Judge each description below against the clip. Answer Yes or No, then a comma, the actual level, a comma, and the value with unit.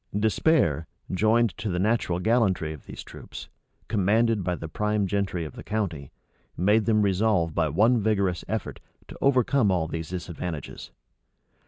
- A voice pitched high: No, low, 100 Hz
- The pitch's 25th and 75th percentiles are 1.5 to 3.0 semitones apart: No, average, 4.3 semitones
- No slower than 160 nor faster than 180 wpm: No, average, 150 wpm